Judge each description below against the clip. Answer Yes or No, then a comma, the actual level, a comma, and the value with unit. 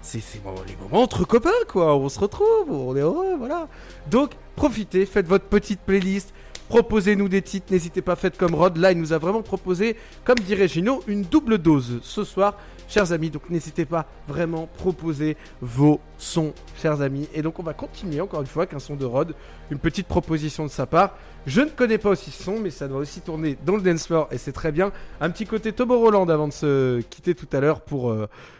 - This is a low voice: No, medium, 175 Hz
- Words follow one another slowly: No, fast, 220 wpm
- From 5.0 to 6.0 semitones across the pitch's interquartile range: Yes, average, 5.3 semitones